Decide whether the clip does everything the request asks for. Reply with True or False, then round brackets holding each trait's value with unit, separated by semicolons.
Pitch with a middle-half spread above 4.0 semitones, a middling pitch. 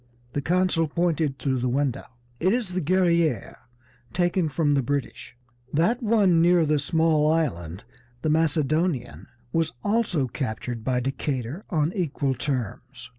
True (4.6 semitones; 155 Hz)